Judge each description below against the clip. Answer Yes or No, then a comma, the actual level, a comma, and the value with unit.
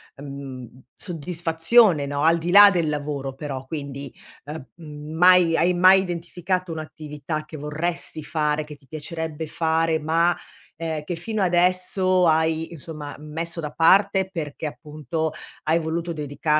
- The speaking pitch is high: No, medium, 160 Hz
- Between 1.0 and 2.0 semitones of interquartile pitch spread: No, narrow, 2.5 semitones